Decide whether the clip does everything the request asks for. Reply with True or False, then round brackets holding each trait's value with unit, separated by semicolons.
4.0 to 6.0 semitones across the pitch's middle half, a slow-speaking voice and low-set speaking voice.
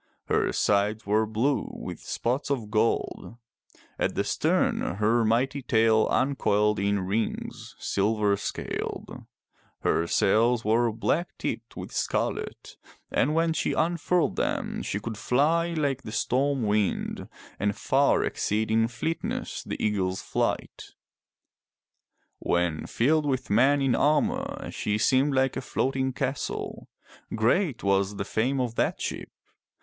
True (4.7 semitones; 130 wpm; 115 Hz)